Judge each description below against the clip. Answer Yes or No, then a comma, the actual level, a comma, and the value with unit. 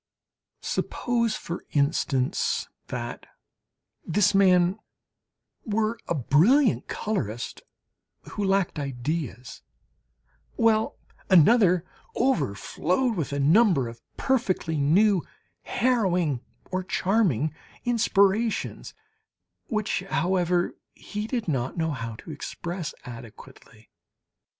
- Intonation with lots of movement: Yes, wide, 7.2 semitones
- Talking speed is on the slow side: Yes, slow, 90 wpm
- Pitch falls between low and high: Yes, medium, 180 Hz